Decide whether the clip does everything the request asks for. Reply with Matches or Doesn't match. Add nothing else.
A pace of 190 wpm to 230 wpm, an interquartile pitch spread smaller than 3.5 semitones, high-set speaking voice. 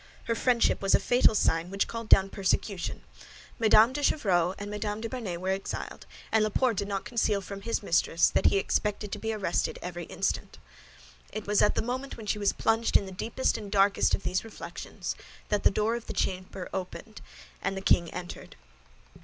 Matches